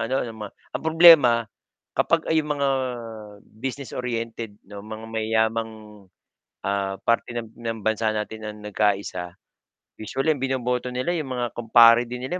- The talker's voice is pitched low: Yes, low, 115 Hz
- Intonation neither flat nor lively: Yes, average, 3.0 semitones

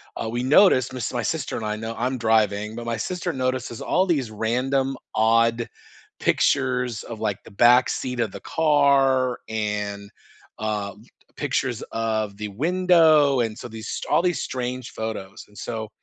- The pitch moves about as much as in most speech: Yes, average, 3.4 semitones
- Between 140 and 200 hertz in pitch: No, low, 120 Hz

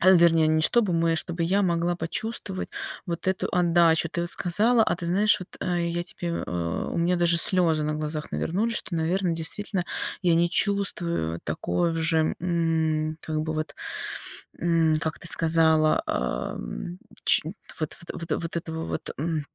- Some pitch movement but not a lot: No, narrow, 1.8 semitones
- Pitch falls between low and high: Yes, medium, 170 Hz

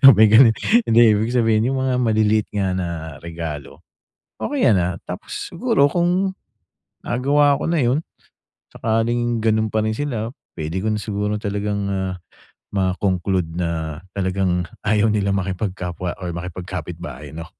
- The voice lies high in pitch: No, low, 105 Hz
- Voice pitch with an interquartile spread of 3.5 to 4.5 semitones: Yes, average, 4.1 semitones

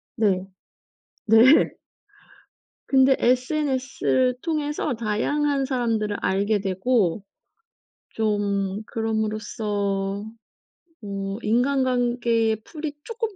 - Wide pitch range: No, average, 4.1 semitones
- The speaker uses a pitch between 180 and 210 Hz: No, high, 225 Hz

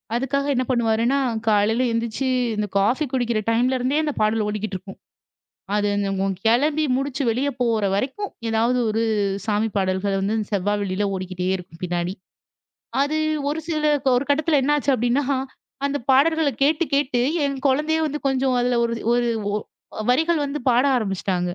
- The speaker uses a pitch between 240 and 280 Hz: Yes, high, 245 Hz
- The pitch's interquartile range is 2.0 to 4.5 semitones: No, average, 5.2 semitones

